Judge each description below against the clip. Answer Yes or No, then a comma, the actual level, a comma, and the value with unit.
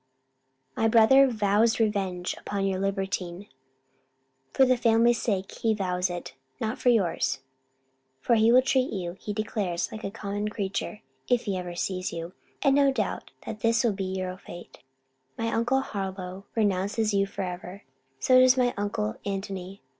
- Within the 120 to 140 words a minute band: No, average, 160 wpm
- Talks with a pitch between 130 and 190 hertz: No, high, 200 Hz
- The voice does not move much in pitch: No, average, 3.3 semitones